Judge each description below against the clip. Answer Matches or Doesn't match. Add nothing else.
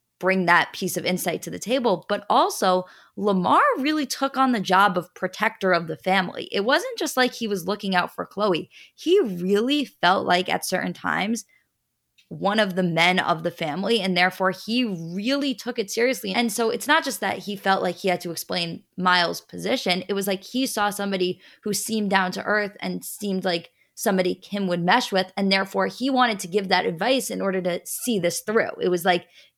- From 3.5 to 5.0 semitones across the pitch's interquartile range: Matches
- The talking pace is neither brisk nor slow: Doesn't match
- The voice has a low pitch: Doesn't match